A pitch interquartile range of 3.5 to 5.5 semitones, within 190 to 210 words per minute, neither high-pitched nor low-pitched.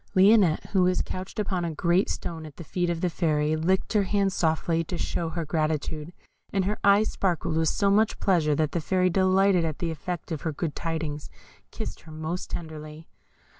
No: average, 3.1 semitones; average, 200 wpm; medium, 170 Hz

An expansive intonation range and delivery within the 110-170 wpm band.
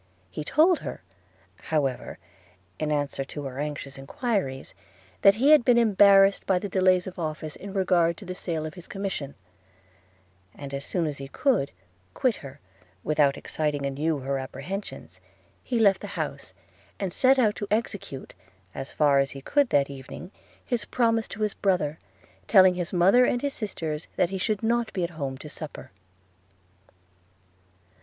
Yes: wide, 6.1 semitones; average, 165 wpm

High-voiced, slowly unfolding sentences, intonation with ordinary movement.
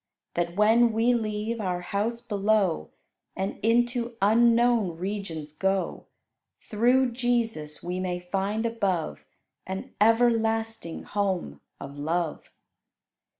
Yes: high, 210 Hz; slow, 105 wpm; average, 4.4 semitones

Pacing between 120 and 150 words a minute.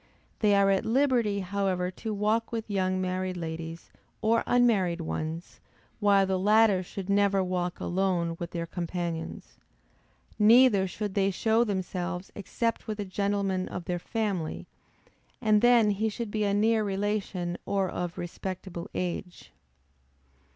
Yes: average, 140 wpm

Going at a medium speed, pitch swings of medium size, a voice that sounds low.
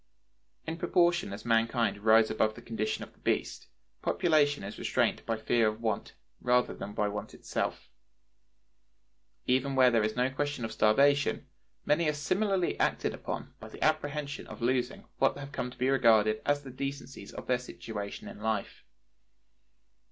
Yes: average, 165 wpm; average, 4.5 semitones; low, 125 Hz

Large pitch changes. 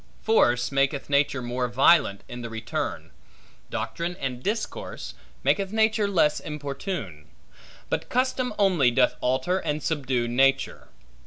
Yes: wide, 7.1 semitones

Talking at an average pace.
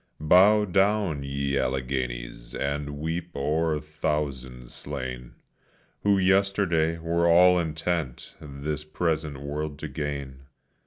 No: slow, 105 wpm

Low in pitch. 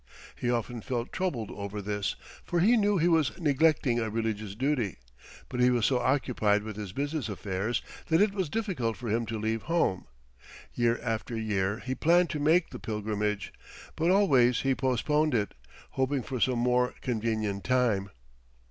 Yes: low, 120 Hz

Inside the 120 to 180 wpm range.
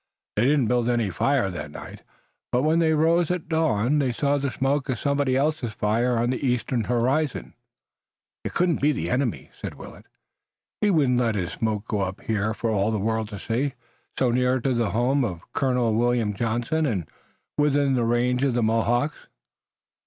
No: average, 190 wpm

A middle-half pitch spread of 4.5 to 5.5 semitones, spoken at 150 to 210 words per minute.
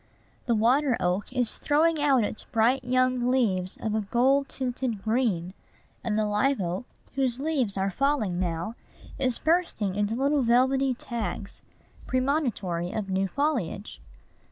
No: average, 4.9 semitones; average, 140 wpm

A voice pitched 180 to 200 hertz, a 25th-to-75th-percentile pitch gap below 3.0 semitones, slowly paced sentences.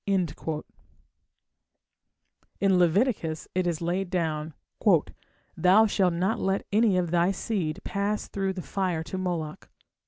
Yes: medium, 185 Hz; narrow, 2.5 semitones; slow, 120 wpm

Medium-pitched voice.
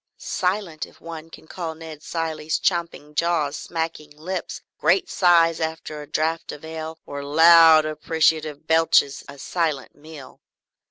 Yes: medium, 160 Hz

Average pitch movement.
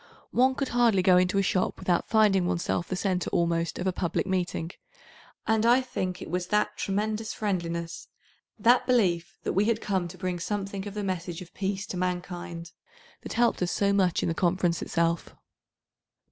Yes: average, 3.0 semitones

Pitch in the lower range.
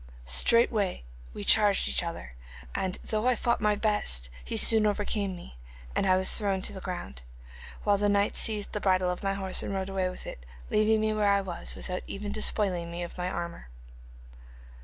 No: high, 195 Hz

